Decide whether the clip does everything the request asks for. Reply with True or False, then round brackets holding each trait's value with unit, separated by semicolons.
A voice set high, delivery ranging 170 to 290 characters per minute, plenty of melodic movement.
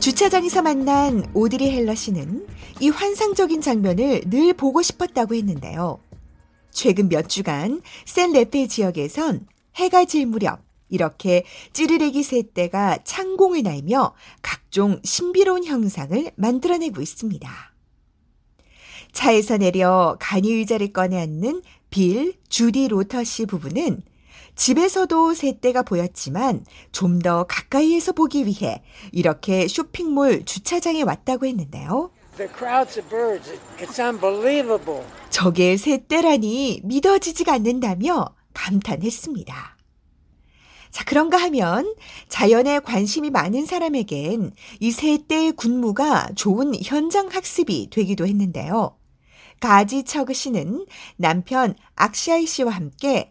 True (245 Hz; 250 characters per minute; 7.8 semitones)